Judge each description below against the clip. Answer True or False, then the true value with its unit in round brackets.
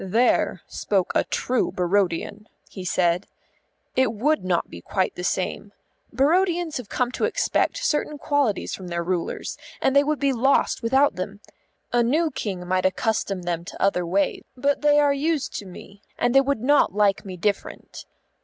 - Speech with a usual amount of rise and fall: False (7.1 semitones)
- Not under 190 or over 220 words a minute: False (170 wpm)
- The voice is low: False (220 Hz)